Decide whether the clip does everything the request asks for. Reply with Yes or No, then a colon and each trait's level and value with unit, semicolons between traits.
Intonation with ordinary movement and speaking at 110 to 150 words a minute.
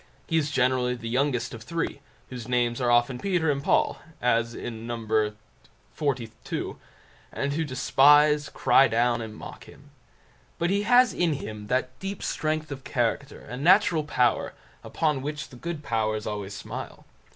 No: average, 4.3 semitones; average, 160 wpm